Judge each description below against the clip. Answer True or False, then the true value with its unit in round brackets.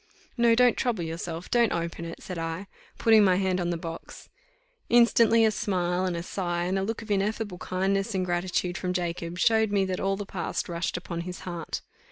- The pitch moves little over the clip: False (3.1 semitones)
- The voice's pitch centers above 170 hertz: True (185 Hz)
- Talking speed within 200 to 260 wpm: True (205 wpm)